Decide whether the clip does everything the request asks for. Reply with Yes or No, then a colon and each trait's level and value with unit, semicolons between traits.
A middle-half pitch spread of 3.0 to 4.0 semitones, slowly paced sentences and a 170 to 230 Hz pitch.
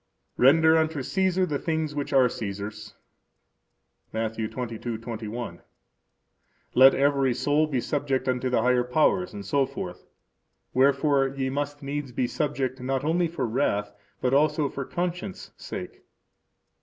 No: average, 3.3 semitones; slow, 125 wpm; low, 135 Hz